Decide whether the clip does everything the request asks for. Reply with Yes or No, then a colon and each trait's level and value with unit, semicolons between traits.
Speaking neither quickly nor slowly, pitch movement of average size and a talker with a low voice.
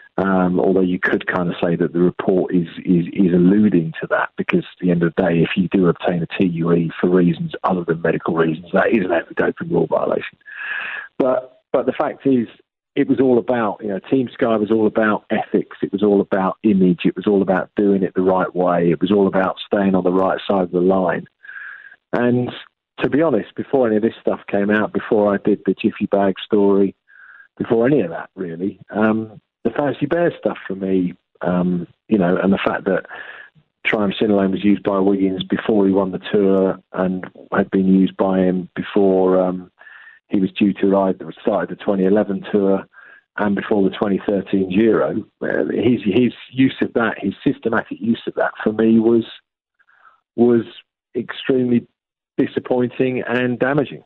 Yes: average, 195 wpm; average, 3.0 semitones; low, 100 Hz